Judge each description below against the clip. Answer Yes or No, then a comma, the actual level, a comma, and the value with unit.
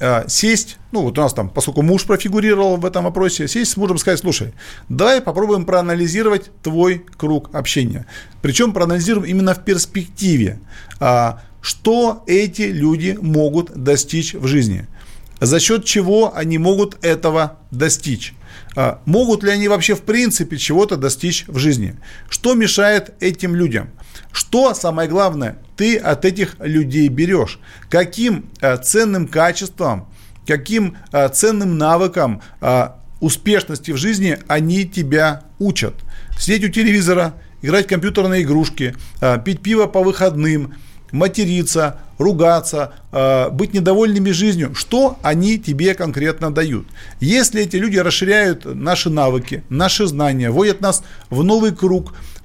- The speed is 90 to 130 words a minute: Yes, average, 125 wpm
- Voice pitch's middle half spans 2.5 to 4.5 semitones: No, wide, 5.5 semitones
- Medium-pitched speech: Yes, medium, 175 Hz